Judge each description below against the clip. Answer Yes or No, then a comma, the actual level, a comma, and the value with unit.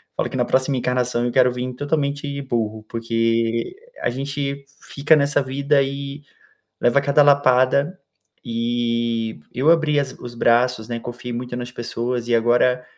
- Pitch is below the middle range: Yes, low, 125 Hz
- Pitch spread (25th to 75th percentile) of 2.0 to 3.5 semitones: Yes, average, 2.9 semitones